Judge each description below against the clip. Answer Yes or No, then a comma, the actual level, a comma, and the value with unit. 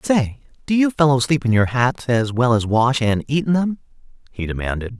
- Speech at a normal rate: No, fast, 215 wpm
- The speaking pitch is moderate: No, low, 130 Hz